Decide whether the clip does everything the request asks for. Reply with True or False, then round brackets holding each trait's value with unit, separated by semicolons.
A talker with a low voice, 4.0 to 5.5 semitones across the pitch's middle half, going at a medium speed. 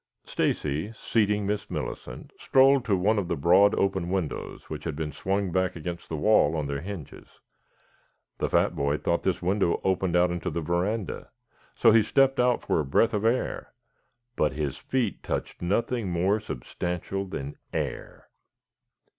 True (95 Hz; 4.3 semitones; 165 wpm)